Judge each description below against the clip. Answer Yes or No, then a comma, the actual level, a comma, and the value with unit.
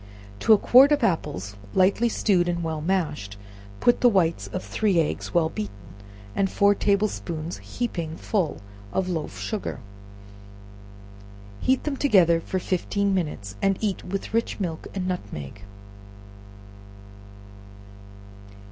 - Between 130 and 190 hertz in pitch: Yes, medium, 185 Hz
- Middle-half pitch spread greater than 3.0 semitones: Yes, average, 4.2 semitones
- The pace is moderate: No, slow, 130 wpm